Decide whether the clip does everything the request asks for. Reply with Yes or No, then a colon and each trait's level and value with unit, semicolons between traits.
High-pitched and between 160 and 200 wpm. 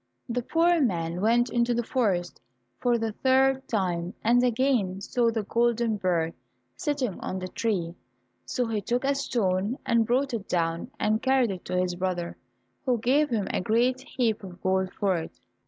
Yes: high, 225 Hz; average, 175 wpm